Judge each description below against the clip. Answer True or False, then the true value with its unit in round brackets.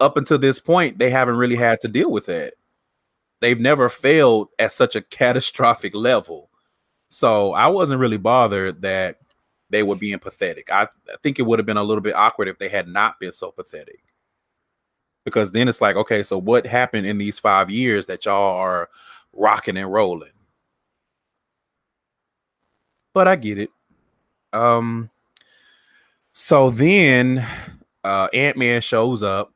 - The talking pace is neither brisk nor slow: True (155 wpm)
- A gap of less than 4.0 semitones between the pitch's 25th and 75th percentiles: False (5.2 semitones)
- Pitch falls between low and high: False (120 Hz)